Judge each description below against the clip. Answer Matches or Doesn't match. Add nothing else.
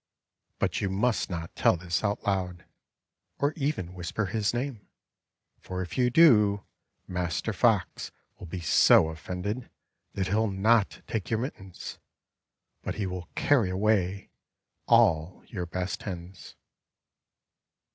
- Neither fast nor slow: Doesn't match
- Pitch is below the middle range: Matches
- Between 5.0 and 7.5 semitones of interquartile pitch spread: Doesn't match